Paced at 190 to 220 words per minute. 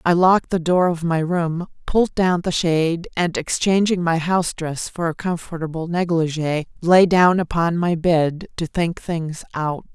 No: average, 175 wpm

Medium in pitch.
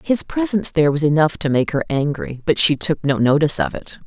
Yes: medium, 160 Hz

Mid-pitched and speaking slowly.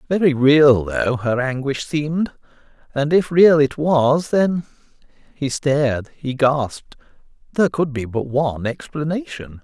Yes: medium, 145 Hz; slow, 125 wpm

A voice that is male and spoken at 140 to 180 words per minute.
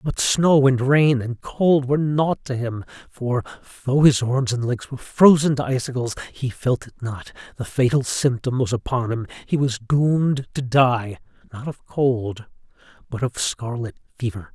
Yes: male; average, 170 wpm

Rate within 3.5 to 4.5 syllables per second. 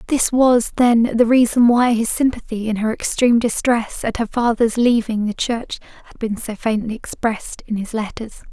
No: 4.8 syllables/s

